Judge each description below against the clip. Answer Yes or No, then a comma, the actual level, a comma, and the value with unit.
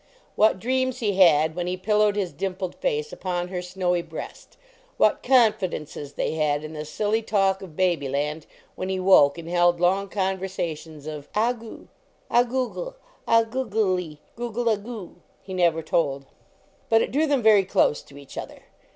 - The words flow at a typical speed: Yes, average, 175 wpm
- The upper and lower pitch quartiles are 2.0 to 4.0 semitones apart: No, average, 5.3 semitones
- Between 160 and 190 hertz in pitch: Yes, medium, 185 Hz